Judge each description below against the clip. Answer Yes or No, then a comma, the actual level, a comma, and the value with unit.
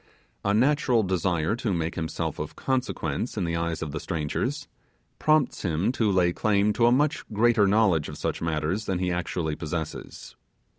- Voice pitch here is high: No, very low, 95 Hz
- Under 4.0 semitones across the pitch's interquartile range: No, average, 5.2 semitones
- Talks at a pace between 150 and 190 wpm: Yes, average, 170 wpm